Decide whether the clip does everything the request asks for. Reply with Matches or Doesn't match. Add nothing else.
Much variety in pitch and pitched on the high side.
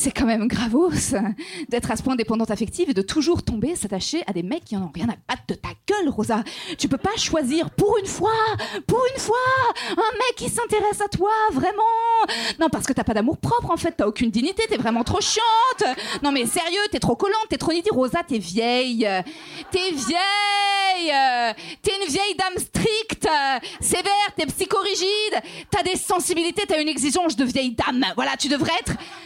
Matches